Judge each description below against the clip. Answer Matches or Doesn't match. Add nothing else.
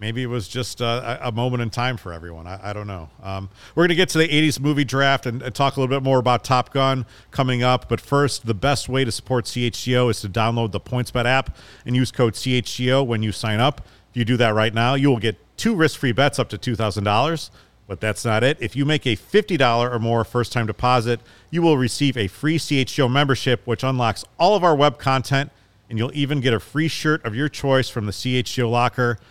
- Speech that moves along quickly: Matches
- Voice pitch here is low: Matches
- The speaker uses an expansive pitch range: Doesn't match